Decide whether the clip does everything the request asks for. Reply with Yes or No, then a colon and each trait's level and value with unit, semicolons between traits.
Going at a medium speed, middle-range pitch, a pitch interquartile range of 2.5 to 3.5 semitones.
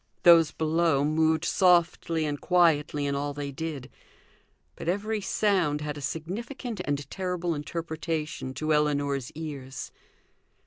No: slow, 125 wpm; medium, 155 Hz; average, 2.9 semitones